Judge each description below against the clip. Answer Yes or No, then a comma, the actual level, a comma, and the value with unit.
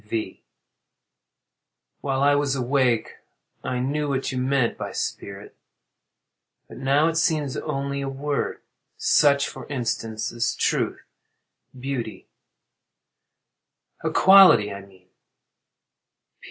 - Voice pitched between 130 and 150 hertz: Yes, low, 135 Hz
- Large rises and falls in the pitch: No, average, 3.6 semitones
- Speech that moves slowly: Yes, slow, 100 wpm